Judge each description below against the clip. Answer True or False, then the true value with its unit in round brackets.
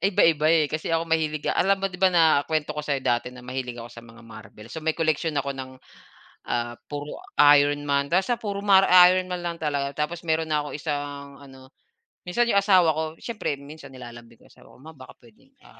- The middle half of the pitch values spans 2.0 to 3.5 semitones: False (3.9 semitones)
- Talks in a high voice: False (150 Hz)